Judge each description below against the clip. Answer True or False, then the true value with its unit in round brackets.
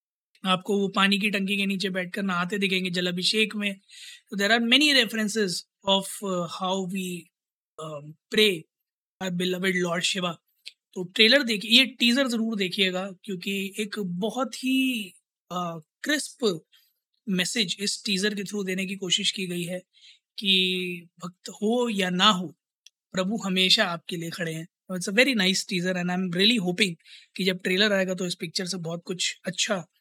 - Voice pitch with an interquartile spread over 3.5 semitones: False (2.8 semitones)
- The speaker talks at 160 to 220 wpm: False (150 wpm)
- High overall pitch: True (195 Hz)